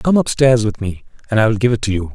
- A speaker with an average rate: No, fast, 335 wpm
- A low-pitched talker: Yes, low, 110 Hz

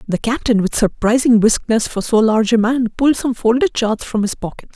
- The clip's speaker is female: Yes, female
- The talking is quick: Yes, fast, 215 wpm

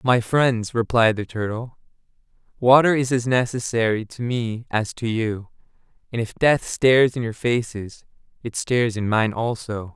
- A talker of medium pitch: No, low, 115 Hz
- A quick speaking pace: No, average, 155 wpm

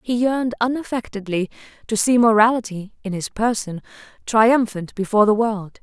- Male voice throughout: No, female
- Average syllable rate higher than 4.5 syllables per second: Yes, 5.0 syllables/s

